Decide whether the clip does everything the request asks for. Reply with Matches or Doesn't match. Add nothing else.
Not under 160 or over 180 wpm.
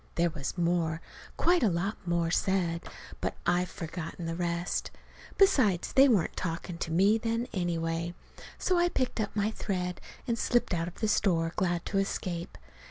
Matches